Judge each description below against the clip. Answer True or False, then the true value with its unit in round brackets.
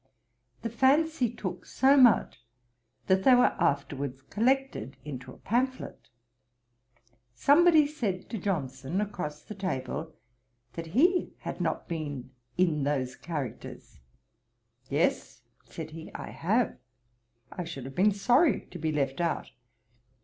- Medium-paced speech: False (125 wpm)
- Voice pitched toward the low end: False (180 Hz)